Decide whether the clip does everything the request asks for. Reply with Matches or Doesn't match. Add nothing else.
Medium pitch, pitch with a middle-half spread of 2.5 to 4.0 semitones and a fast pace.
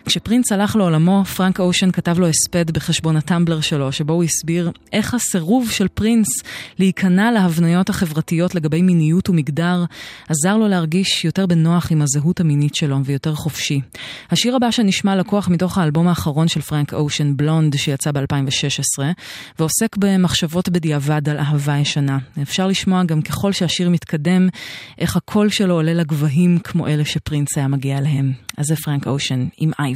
Matches